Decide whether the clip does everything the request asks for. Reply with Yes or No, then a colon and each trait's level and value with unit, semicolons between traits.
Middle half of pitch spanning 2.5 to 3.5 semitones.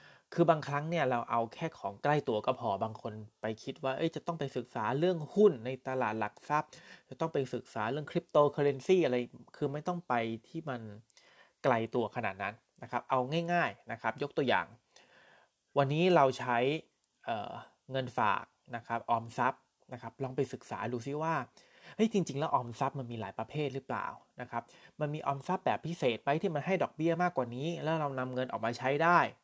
No: average, 5.0 semitones